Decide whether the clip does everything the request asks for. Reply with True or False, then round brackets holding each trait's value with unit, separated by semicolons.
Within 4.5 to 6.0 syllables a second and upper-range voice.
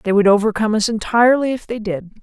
False (6.6 syllables/s; 215 Hz)